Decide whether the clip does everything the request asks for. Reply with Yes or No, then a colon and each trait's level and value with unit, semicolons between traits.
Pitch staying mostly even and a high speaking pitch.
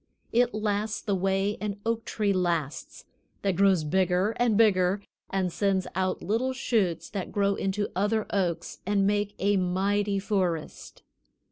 Yes: narrow, 2.0 semitones; high, 200 Hz